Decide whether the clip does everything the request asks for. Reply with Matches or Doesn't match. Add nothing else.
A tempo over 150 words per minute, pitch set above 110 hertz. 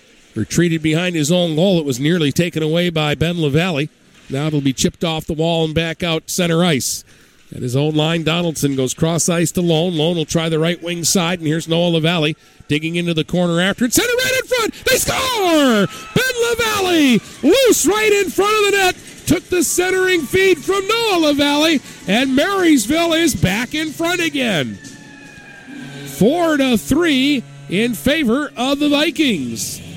Matches